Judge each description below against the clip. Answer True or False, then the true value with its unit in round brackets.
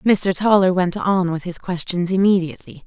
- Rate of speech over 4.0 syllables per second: True (5.0 syllables/s)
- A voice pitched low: False (185 Hz)